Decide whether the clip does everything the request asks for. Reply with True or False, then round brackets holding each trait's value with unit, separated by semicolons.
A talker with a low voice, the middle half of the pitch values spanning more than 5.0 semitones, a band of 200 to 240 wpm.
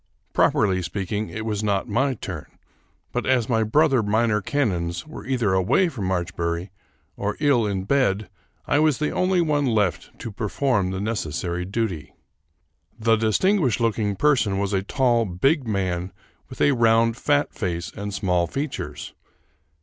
False (110 Hz; 5.5 semitones; 150 wpm)